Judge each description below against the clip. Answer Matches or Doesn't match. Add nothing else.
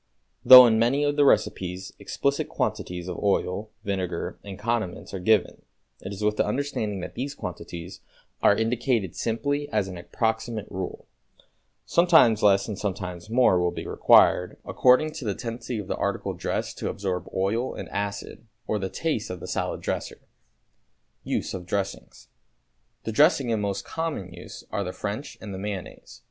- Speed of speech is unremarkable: Matches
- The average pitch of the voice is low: Matches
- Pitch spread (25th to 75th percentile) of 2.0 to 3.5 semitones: Doesn't match